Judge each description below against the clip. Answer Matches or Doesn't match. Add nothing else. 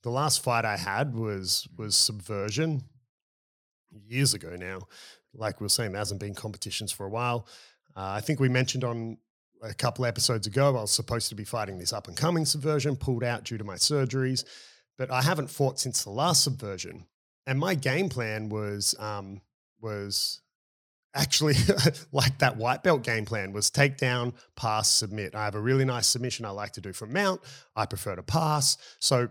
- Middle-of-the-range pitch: Doesn't match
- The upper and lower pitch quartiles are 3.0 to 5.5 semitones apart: Matches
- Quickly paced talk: Doesn't match